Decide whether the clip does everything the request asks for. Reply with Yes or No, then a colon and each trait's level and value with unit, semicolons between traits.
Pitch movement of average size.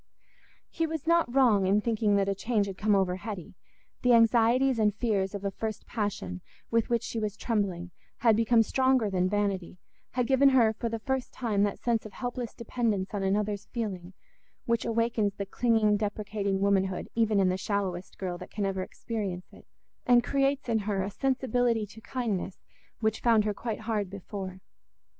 Yes: average, 3.0 semitones